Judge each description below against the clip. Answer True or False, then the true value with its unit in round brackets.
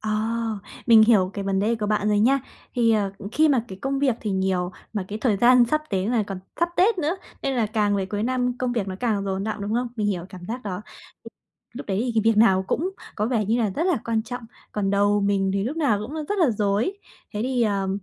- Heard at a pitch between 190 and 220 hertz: True (215 Hz)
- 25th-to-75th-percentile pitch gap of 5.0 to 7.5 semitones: False (3.8 semitones)